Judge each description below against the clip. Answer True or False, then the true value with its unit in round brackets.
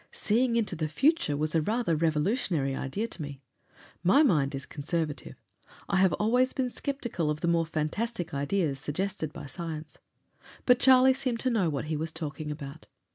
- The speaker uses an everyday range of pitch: False (7.4 semitones)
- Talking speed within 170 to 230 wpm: True (175 wpm)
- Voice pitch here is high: False (165 Hz)